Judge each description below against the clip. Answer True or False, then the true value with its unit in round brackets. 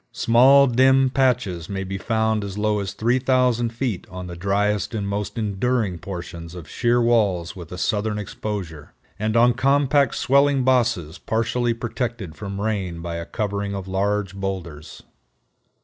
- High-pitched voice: False (105 Hz)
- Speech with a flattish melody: False (4.2 semitones)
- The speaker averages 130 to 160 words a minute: True (150 wpm)